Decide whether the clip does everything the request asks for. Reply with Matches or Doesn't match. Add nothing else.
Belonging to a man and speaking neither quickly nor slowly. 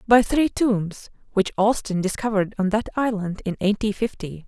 Doesn't match